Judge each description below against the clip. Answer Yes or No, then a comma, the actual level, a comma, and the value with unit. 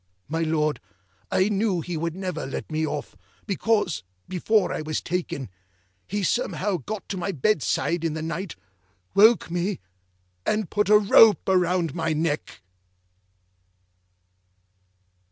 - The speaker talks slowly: Yes, slow, 130 wpm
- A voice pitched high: No, medium, 175 Hz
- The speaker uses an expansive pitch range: No, average, 4.1 semitones